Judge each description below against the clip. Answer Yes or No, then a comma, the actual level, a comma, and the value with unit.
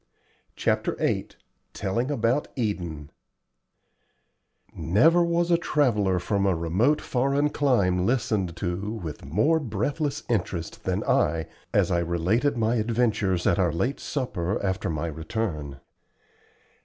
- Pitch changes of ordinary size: No, wide, 6.9 semitones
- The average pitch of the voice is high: No, low, 105 Hz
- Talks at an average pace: No, slow, 120 wpm